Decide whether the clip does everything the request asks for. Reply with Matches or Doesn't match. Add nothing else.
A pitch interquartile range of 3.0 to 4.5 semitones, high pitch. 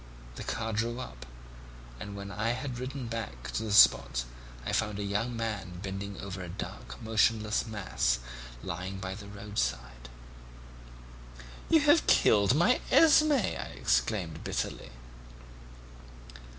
Doesn't match